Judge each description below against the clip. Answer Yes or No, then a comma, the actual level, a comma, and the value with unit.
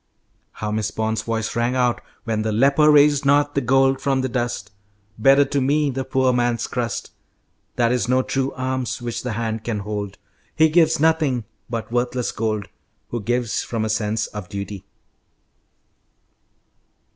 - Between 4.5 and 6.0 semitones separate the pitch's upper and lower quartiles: No, average, 3.4 semitones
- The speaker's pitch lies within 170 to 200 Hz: No, low, 120 Hz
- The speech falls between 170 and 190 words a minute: No, average, 160 wpm